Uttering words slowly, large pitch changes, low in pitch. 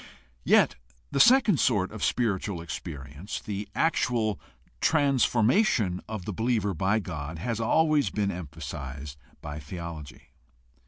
Yes: slow, 120 wpm; wide, 7.0 semitones; low, 100 Hz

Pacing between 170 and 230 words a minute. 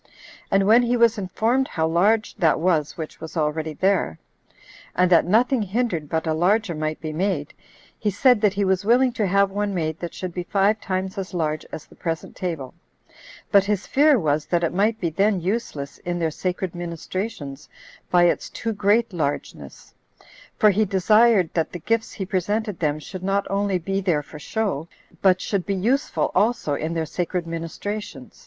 Yes: average, 185 wpm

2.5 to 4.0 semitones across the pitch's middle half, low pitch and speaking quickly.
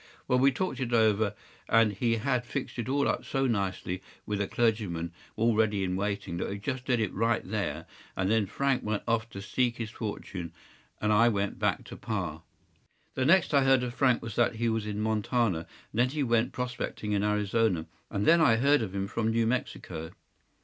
Yes: average, 3.4 semitones; low, 110 Hz; fast, 210 wpm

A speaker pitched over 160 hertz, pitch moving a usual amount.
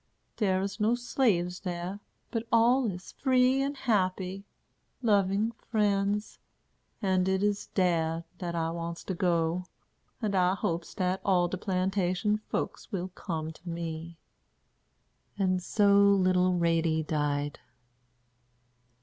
Yes: medium, 185 Hz; average, 3.1 semitones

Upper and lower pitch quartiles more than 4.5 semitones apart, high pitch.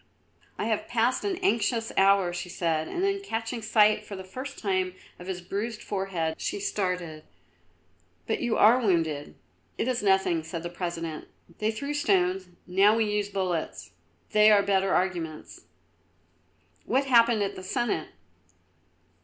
No: average, 4.1 semitones; high, 200 Hz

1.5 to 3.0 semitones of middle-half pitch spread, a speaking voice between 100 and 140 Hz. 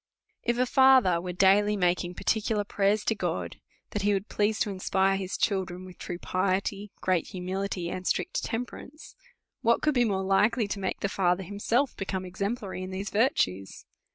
No: narrow, 2.4 semitones; high, 195 Hz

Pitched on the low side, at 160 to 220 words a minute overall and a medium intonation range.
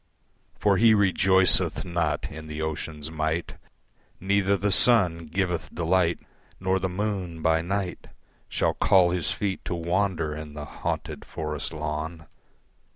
No: very low, 85 Hz; slow, 135 wpm; average, 3.3 semitones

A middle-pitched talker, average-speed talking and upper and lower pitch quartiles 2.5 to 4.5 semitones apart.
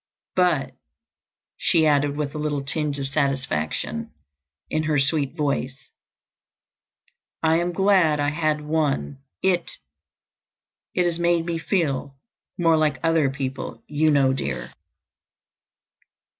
No: medium, 150 Hz; slow, 115 wpm; average, 2.8 semitones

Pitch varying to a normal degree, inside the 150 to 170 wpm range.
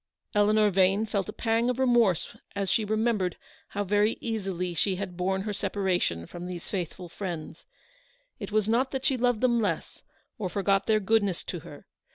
No: average, 3.2 semitones; average, 180 wpm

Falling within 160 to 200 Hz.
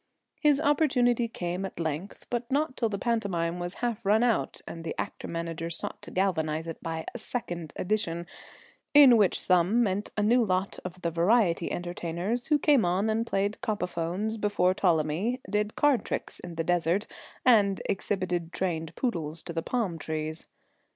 Yes: high, 190 Hz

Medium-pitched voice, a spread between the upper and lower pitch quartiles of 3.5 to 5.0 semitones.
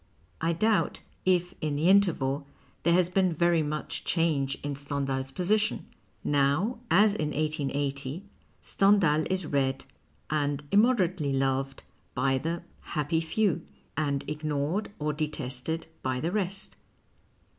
Yes: medium, 155 Hz; average, 4.4 semitones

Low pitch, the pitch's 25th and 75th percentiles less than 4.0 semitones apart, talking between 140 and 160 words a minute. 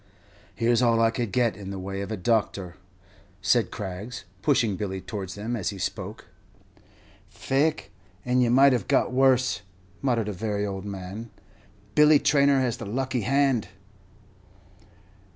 No: low, 115 Hz; average, 4.3 semitones; average, 150 wpm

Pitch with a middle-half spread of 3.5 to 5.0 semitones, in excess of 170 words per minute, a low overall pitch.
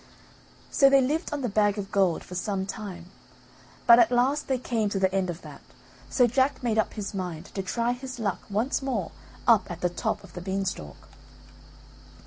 No: average, 4.5 semitones; average, 195 wpm; high, 210 Hz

